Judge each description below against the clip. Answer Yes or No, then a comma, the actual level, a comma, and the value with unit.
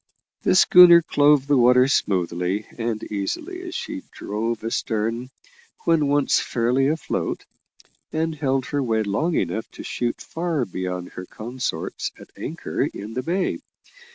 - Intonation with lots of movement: Yes, wide, 5.9 semitones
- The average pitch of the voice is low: Yes, low, 125 Hz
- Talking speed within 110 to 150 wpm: Yes, average, 140 wpm